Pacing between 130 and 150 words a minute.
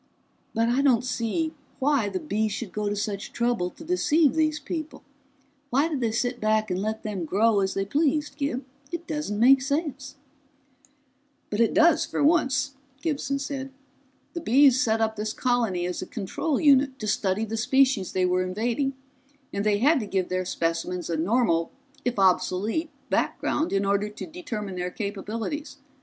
No: average, 175 wpm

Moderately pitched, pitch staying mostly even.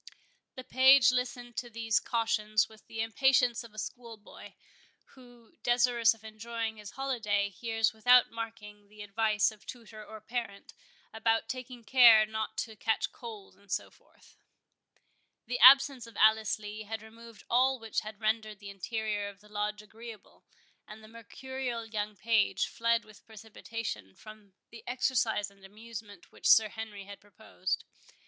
No: high, 220 Hz; narrow, 1.9 semitones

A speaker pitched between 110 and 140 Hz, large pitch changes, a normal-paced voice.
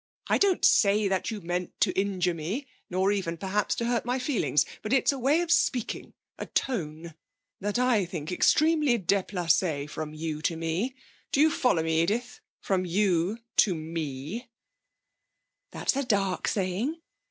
No: high, 195 Hz; wide, 6.6 semitones; average, 160 wpm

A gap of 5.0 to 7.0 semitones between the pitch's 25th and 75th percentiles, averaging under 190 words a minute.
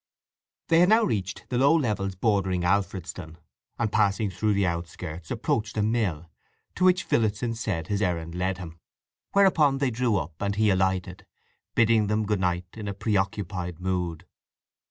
No: average, 3.7 semitones; average, 160 wpm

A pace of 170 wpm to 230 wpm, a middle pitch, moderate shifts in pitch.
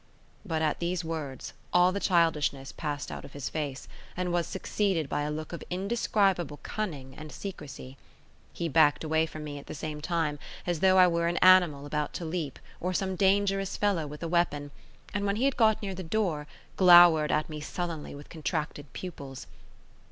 Yes: average, 190 wpm; medium, 165 Hz; average, 3.8 semitones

